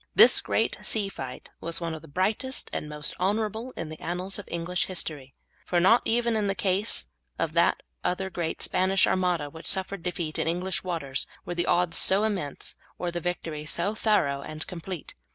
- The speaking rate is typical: Yes, average, 190 wpm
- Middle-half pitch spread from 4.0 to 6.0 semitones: No, average, 3.2 semitones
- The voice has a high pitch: No, medium, 180 Hz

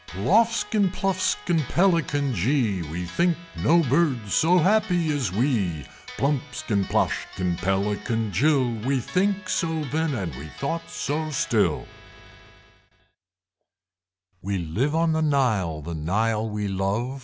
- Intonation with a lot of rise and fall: Yes, wide, 8.6 semitones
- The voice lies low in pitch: Yes, low, 130 Hz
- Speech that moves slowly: Yes, slow, 120 wpm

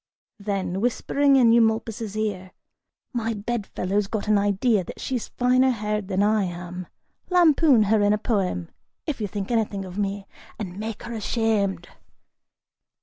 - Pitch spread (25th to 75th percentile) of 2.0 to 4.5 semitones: Yes, average, 2.8 semitones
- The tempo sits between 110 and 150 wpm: Yes, average, 145 wpm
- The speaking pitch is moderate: No, high, 210 Hz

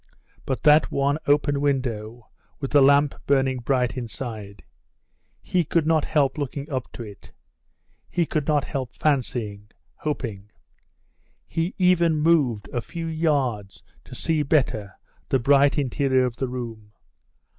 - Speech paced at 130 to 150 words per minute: Yes, slow, 135 wpm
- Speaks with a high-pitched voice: No, low, 135 Hz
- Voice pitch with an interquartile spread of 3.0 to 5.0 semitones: Yes, average, 3.9 semitones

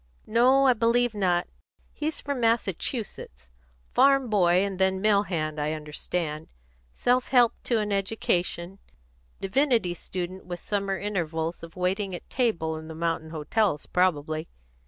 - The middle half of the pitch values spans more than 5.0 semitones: Yes, wide, 5.5 semitones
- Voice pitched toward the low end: No, high, 190 Hz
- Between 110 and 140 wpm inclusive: Yes, slow, 135 wpm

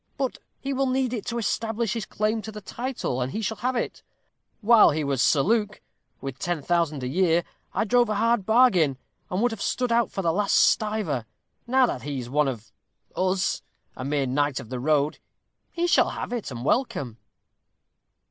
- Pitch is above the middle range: Yes, high, 195 Hz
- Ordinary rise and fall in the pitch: No, wide, 8.5 semitones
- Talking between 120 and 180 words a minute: No, average, 195 wpm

